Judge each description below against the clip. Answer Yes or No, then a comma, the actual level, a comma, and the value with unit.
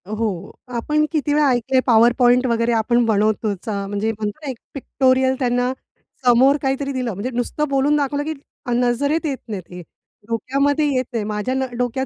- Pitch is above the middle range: Yes, high, 245 Hz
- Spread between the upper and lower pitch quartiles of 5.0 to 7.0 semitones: No, average, 3.4 semitones